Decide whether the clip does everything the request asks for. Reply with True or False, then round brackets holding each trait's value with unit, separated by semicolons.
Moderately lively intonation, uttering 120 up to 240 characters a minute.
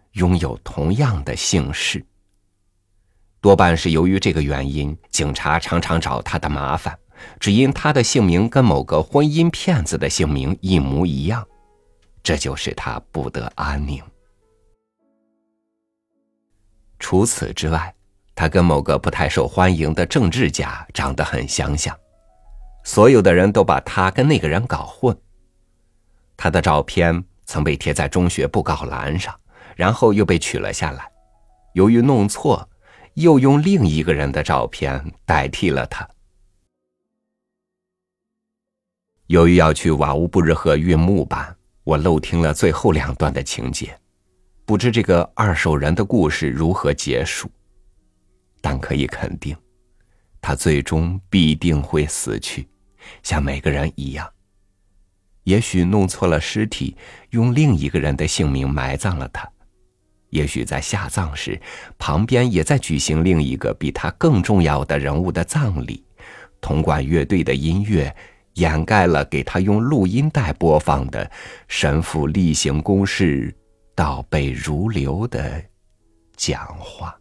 True (4.5 semitones; 200 characters per minute)